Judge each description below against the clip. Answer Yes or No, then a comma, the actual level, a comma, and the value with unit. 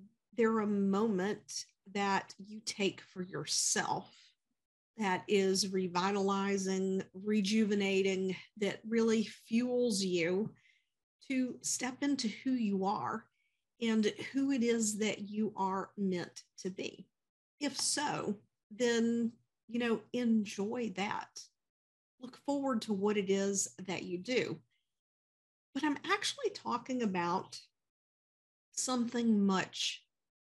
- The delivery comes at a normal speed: No, slow, 110 wpm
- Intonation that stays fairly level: No, average, 3.4 semitones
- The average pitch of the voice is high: Yes, high, 210 Hz